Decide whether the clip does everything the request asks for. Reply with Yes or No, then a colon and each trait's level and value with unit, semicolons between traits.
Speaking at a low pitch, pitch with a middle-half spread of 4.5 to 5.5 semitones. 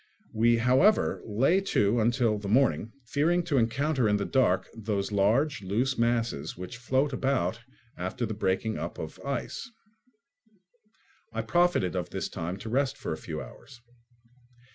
Yes: low, 115 Hz; average, 5.0 semitones